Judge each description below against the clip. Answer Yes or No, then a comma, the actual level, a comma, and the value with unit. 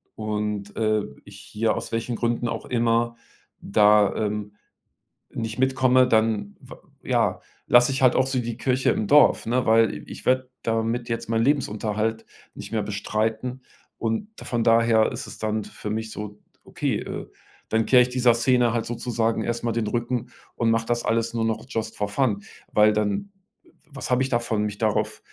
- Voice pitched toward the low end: Yes, low, 115 Hz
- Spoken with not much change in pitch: Yes, narrow, 2.1 semitones